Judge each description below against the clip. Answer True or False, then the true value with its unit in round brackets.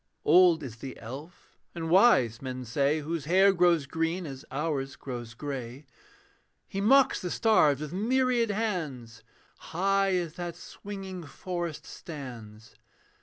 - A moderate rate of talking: False (130 wpm)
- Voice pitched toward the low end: False (165 Hz)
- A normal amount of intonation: False (5.7 semitones)